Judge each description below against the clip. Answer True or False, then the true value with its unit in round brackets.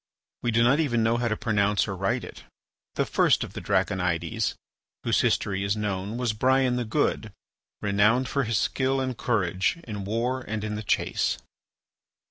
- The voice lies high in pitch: False (110 Hz)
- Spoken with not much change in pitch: False (3.4 semitones)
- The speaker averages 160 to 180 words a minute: True (175 wpm)